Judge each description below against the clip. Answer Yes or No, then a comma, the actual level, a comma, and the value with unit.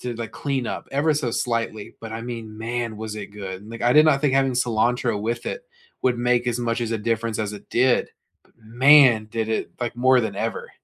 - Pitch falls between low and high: No, low, 115 Hz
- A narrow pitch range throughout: Yes, narrow, 2.1 semitones